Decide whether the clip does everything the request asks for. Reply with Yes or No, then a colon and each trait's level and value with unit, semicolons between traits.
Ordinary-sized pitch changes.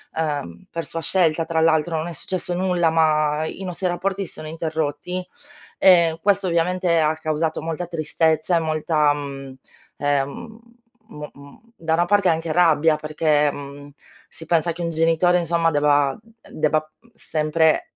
No: narrow, 2.2 semitones